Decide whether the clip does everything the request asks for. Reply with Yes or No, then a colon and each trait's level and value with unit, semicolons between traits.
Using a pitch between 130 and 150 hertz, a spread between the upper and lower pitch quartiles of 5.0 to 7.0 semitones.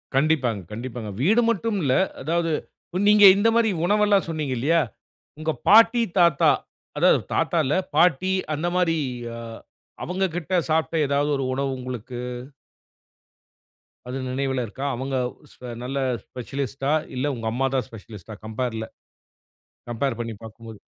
Yes: medium, 140 Hz; wide, 5.4 semitones